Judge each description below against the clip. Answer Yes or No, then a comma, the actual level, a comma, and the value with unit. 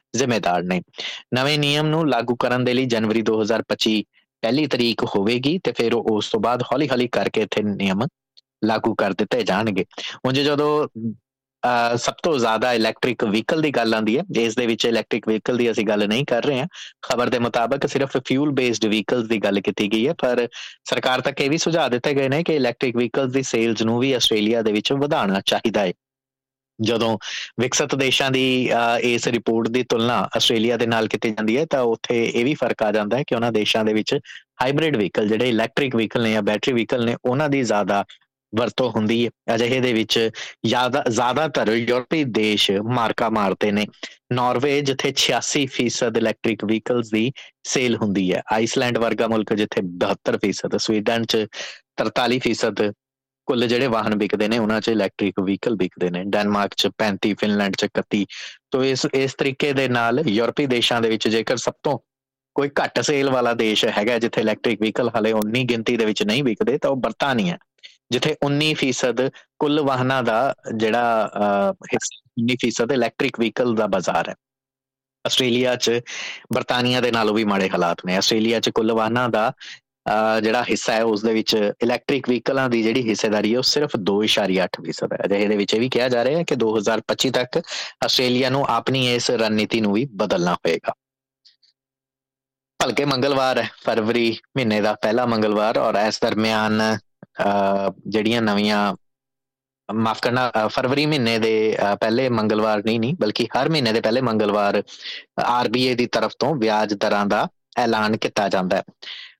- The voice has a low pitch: Yes, low, 115 Hz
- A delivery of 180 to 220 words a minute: No, average, 165 wpm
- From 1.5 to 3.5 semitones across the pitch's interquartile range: Yes, average, 3.2 semitones